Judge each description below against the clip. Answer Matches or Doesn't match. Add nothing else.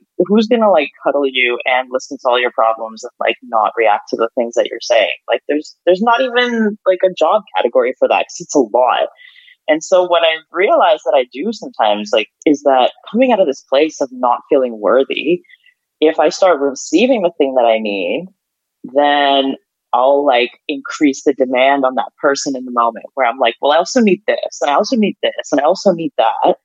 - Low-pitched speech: Doesn't match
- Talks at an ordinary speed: Doesn't match